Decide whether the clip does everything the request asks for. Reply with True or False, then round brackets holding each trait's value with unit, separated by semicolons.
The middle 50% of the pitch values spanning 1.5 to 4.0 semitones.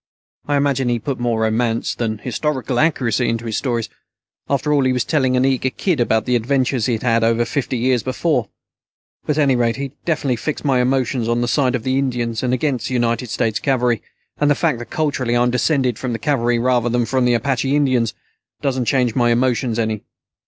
True (2.4 semitones)